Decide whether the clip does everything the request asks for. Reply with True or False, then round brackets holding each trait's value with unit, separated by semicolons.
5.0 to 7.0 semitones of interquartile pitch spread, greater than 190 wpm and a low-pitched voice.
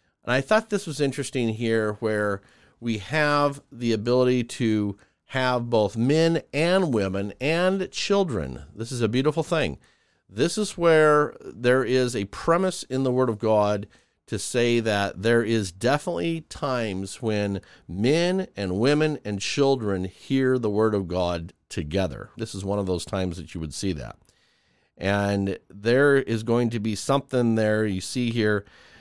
False (5.6 semitones; 160 wpm; 115 Hz)